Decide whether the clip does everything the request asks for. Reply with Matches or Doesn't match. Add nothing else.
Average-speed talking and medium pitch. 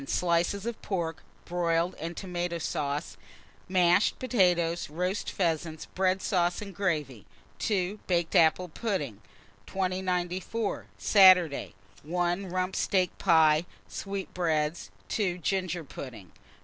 Doesn't match